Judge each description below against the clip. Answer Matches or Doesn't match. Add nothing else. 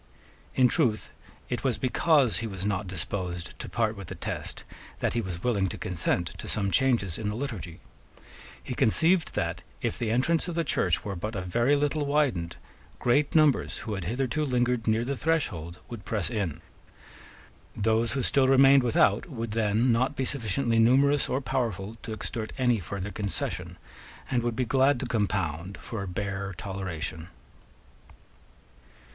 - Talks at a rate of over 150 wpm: Matches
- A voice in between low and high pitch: Doesn't match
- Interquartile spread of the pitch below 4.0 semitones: Doesn't match